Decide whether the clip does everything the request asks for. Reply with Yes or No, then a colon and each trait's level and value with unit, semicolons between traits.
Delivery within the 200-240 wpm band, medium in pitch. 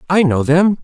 Yes: fast, 215 wpm; medium, 165 Hz